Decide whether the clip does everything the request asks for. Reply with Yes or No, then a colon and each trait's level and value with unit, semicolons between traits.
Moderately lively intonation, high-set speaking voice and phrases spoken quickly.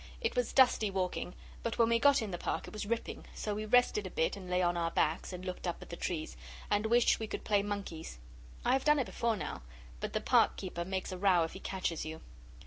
Yes: average, 4.3 semitones; high, 195 Hz; fast, 250 wpm